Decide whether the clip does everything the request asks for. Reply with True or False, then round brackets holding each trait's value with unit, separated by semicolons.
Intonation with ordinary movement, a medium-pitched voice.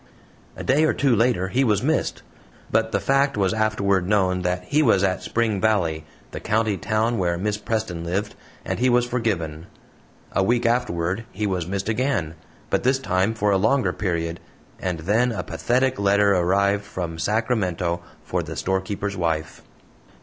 False (4.0 semitones; 100 Hz)